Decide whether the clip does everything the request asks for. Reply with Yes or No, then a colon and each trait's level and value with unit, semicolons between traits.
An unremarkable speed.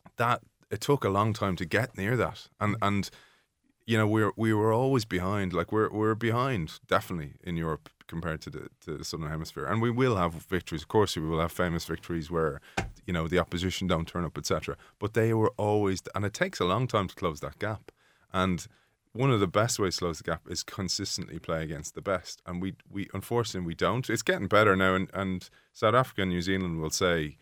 No: fast, 225 wpm